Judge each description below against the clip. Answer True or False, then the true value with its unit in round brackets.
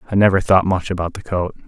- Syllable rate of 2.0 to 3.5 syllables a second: False (6.7 syllables/s)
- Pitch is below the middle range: True (90 Hz)